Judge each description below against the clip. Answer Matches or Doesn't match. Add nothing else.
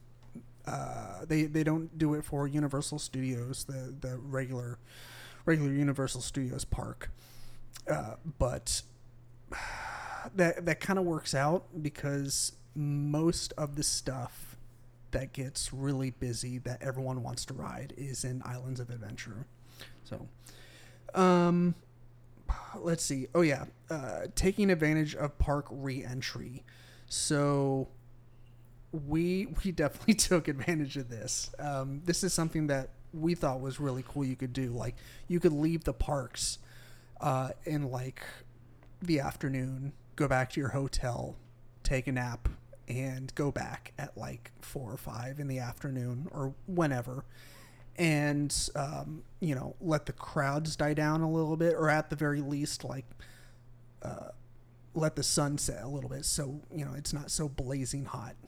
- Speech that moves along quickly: Doesn't match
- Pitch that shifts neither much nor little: Matches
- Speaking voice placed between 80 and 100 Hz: Doesn't match